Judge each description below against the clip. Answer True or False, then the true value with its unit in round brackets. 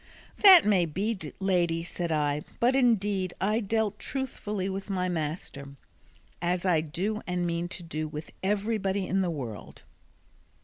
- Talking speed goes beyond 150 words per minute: False (145 wpm)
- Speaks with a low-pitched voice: False (185 Hz)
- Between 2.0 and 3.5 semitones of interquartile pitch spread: False (3.9 semitones)